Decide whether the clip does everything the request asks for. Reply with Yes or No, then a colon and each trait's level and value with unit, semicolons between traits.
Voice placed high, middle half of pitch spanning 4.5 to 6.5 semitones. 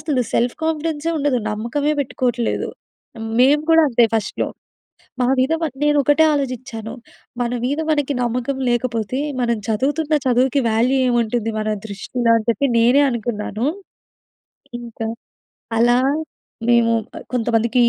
No: high, 245 Hz; average, 3.5 semitones